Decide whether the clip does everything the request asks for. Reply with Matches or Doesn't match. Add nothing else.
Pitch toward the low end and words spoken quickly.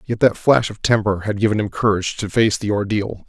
Matches